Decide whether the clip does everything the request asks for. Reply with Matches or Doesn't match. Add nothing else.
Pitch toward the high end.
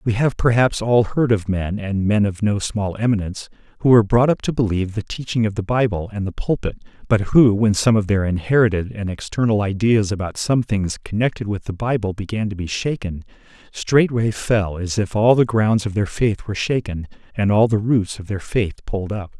Doesn't match